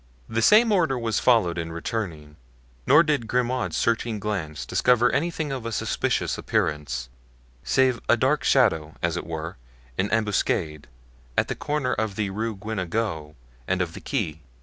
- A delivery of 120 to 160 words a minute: Yes, average, 155 wpm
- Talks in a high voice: No, low, 110 Hz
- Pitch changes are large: Yes, wide, 7.0 semitones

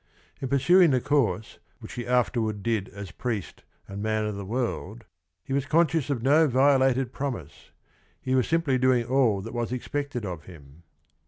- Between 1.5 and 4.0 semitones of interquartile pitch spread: No, average, 4.4 semitones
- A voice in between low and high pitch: No, low, 125 Hz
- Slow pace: No, average, 175 wpm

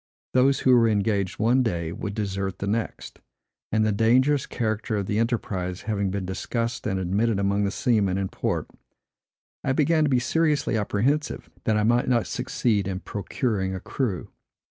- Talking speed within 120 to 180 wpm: Yes, average, 170 wpm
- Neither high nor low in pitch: No, low, 110 Hz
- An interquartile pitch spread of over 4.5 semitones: No, average, 3.8 semitones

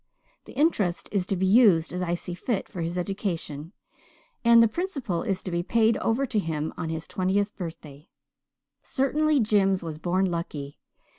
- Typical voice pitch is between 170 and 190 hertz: Yes, medium, 185 Hz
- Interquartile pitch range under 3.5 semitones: No, average, 4.9 semitones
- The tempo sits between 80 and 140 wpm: No, average, 170 wpm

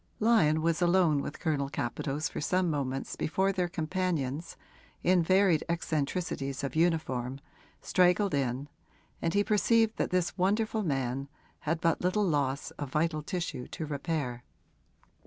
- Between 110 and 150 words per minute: Yes, average, 140 wpm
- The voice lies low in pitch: No, medium, 160 Hz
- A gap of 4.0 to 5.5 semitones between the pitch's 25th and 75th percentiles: Yes, average, 4.6 semitones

